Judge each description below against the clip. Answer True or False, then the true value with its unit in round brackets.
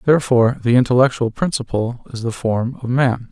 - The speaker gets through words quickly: False (165 wpm)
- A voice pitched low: True (125 Hz)